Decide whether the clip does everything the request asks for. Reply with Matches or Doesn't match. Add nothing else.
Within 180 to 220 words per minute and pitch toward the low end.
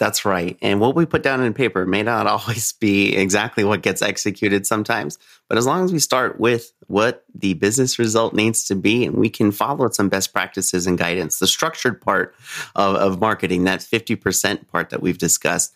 Matches